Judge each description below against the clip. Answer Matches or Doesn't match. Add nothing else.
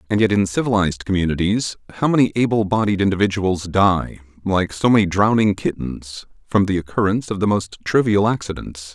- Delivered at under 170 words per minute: Matches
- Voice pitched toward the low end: Matches